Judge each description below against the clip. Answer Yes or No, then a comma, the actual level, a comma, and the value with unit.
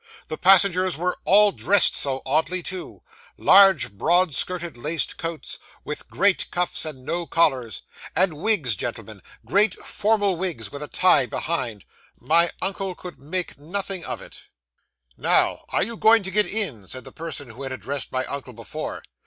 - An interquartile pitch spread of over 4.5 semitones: Yes, wide, 5.5 semitones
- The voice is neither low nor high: Yes, medium, 170 Hz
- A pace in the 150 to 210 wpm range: Yes, average, 160 wpm